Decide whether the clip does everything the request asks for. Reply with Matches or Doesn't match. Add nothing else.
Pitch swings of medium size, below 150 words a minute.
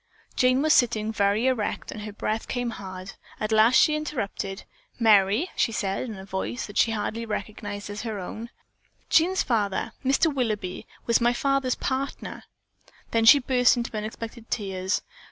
Doesn't match